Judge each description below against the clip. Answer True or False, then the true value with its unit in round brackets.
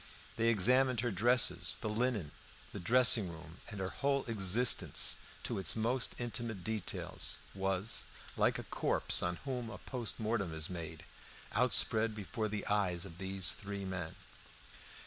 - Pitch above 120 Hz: False (105 Hz)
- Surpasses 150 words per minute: False (145 wpm)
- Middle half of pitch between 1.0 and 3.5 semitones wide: False (4.0 semitones)